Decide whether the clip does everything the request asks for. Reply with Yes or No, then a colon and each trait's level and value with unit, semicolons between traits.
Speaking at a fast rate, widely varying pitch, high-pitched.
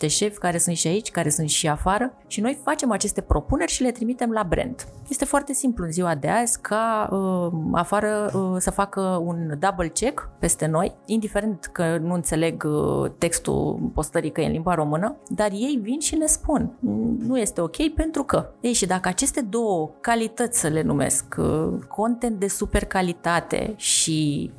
Yes: fast, 180 wpm; wide, 5.8 semitones; high, 205 Hz